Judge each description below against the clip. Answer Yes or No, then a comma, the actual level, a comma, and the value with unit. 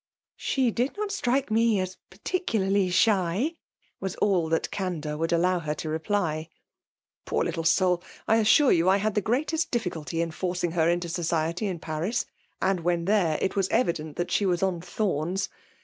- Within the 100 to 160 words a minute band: No, average, 180 wpm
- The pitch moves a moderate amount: Yes, average, 4.3 semitones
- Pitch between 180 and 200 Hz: Yes, medium, 185 Hz